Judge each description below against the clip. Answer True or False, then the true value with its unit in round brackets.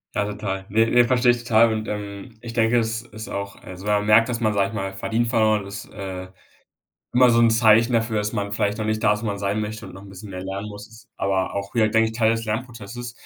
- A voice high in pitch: False (110 Hz)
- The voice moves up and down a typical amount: False (2.2 semitones)